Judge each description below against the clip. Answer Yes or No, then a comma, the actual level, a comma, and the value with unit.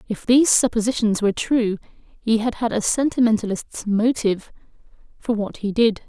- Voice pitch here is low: No, high, 220 Hz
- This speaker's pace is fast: No, average, 150 wpm